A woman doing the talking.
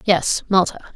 Yes: female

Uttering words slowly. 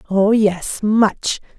Yes: slow, 115 wpm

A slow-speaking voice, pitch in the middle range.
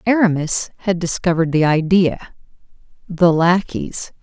Yes: slow, 100 wpm; medium, 175 Hz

